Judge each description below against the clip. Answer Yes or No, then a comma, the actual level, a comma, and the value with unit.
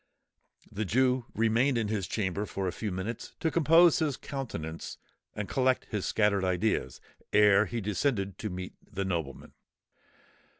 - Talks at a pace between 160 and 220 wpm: No, average, 140 wpm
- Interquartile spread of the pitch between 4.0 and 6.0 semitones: Yes, average, 4.8 semitones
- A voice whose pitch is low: Yes, low, 105 Hz